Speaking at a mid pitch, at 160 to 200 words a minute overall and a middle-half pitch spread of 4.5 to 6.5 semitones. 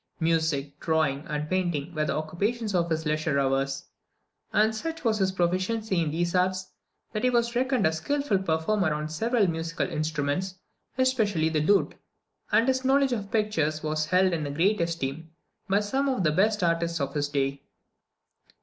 Yes: medium, 170 Hz; average, 170 wpm; wide, 5.5 semitones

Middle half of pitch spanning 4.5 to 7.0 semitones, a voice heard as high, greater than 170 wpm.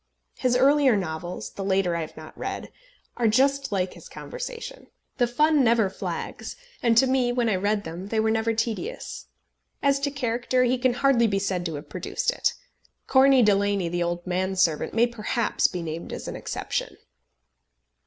Yes: wide, 5.4 semitones; high, 225 Hz; average, 180 wpm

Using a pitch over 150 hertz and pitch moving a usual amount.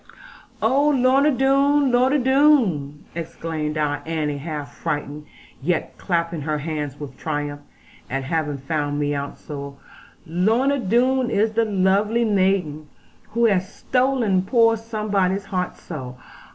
No: medium, 185 Hz; wide, 7.9 semitones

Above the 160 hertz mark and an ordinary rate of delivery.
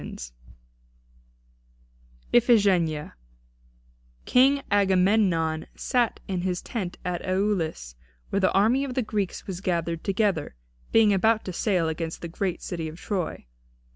No: high, 190 Hz; slow, 125 wpm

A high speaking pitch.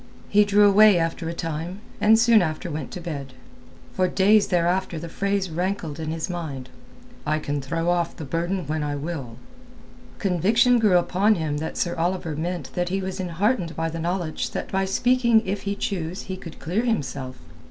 No: medium, 175 Hz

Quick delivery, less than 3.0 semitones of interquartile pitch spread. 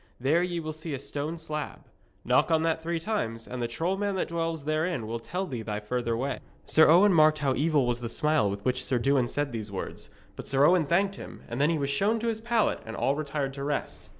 No: fast, 245 wpm; average, 4.9 semitones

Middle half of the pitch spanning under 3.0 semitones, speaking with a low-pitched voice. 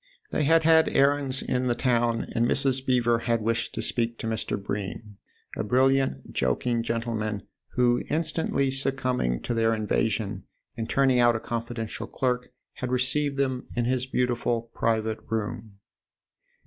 Yes: narrow, 2.6 semitones; low, 120 Hz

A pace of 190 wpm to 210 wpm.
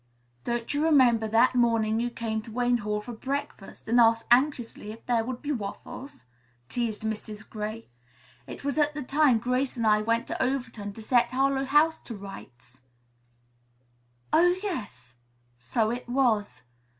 No: average, 160 wpm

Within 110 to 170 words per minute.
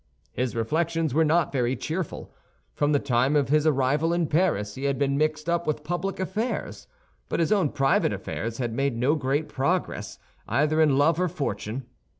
No: average, 180 wpm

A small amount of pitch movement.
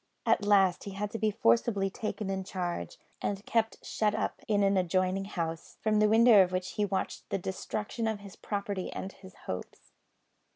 Yes: narrow, 2.1 semitones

